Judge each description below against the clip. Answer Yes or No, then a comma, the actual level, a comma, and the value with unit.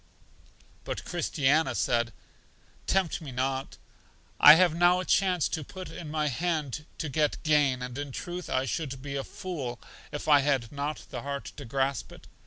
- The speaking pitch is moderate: Yes, medium, 145 Hz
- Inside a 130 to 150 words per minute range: No, average, 170 wpm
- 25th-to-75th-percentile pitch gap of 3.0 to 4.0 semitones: Yes, average, 3.6 semitones